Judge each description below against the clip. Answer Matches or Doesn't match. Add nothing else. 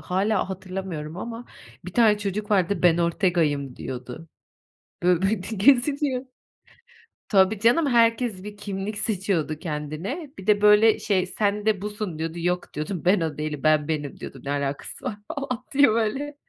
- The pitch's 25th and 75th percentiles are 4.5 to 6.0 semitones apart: Matches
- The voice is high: Matches